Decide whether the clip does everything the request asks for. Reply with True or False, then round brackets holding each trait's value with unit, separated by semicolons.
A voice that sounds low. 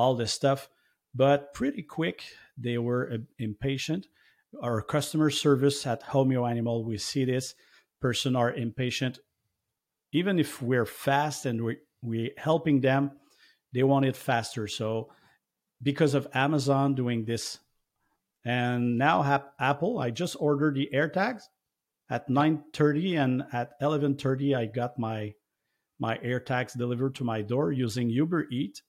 True (130 Hz)